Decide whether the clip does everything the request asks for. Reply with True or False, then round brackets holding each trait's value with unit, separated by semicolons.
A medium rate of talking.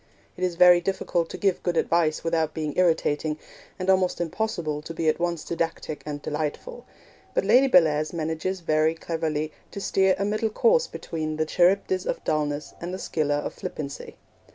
True (175 wpm)